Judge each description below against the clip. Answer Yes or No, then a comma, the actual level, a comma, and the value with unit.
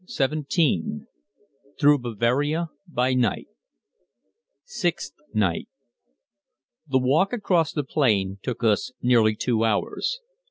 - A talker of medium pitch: No, low, 130 Hz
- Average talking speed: No, slow, 110 wpm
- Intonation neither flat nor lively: No, wide, 5.8 semitones